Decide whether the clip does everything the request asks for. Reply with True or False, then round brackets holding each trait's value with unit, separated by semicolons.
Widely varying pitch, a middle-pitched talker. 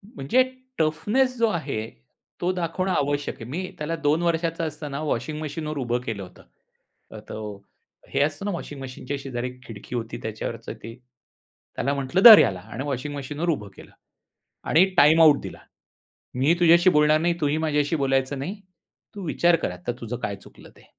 False (4.3 semitones; 145 Hz)